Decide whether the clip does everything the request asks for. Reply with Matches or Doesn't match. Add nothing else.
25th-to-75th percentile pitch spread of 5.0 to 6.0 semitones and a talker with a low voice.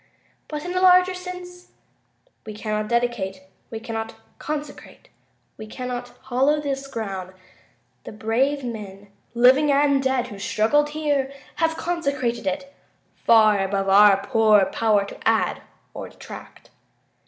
Doesn't match